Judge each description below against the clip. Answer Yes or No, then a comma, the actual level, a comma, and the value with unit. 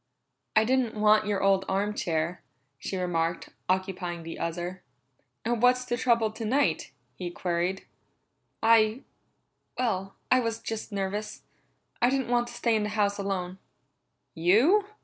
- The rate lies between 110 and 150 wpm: Yes, average, 140 wpm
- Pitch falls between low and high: No, high, 210 Hz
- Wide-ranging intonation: No, average, 4.1 semitones